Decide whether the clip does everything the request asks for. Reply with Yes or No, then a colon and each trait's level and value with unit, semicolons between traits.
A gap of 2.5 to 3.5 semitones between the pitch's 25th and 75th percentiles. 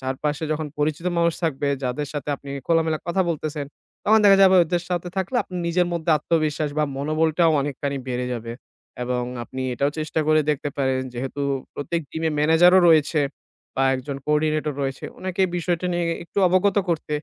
Yes: average, 3.2 semitones